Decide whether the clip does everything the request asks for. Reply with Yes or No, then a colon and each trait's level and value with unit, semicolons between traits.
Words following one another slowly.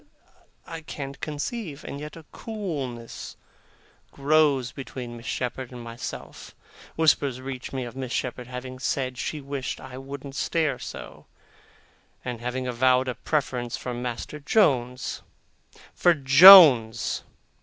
Yes: slow, 125 wpm